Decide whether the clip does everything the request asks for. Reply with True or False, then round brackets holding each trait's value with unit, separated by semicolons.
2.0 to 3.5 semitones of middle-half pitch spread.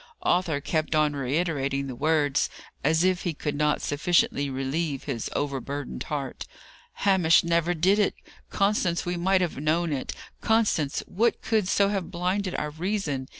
False (4.2 semitones)